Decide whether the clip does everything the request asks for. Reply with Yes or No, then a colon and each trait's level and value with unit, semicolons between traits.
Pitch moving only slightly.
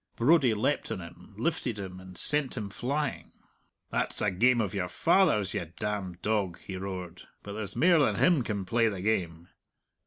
No: average, 5.3 semitones